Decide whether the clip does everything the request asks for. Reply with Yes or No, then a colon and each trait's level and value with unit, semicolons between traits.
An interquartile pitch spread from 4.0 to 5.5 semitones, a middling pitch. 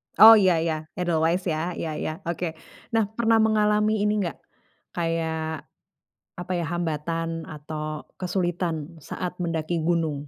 No: narrow, 2.4 semitones; medium, 170 Hz